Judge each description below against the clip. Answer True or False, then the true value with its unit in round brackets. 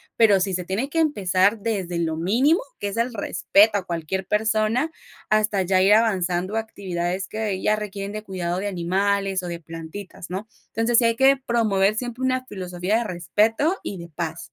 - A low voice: False (200 Hz)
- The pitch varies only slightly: False (3.6 semitones)